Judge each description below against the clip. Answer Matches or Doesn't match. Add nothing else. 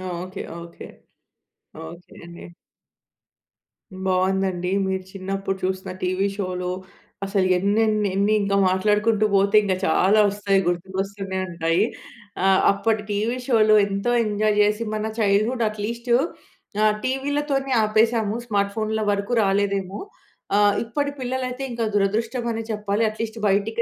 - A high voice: Matches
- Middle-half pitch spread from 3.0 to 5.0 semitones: Doesn't match